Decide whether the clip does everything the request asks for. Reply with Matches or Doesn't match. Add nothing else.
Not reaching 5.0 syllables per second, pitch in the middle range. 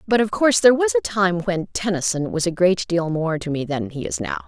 Doesn't match